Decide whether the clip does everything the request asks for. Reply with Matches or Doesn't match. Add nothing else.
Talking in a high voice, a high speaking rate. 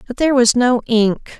Matches